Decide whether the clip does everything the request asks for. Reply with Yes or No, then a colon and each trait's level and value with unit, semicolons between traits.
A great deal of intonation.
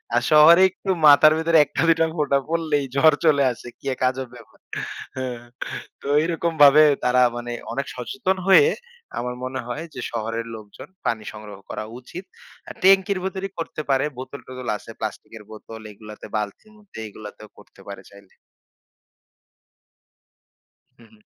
Yes: wide, 6.3 semitones